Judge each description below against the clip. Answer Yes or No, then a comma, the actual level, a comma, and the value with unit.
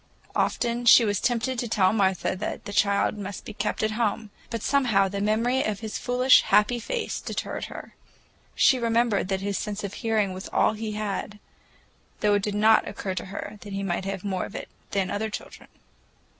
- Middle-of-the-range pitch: No, high, 210 Hz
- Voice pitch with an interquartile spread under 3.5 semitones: Yes, narrow, 2.4 semitones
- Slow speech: No, average, 200 wpm